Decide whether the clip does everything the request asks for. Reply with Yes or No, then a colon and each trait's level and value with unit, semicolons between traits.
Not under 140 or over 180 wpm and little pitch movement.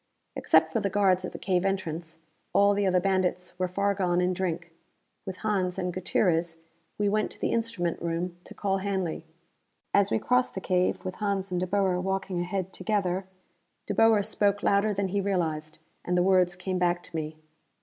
No: average, 190 wpm; narrow, 2.0 semitones